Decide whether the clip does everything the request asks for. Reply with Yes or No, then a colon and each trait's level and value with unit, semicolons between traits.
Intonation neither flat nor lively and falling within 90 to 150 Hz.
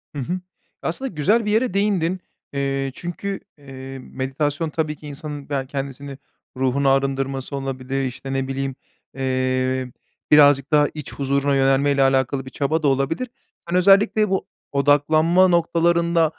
Yes: average, 3.7 semitones; medium, 140 Hz